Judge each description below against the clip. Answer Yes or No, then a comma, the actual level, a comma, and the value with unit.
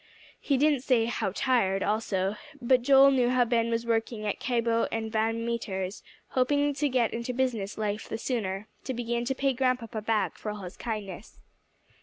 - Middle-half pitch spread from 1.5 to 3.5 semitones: Yes, average, 2.9 semitones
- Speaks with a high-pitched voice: Yes, high, 230 Hz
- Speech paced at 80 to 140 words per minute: No, average, 180 wpm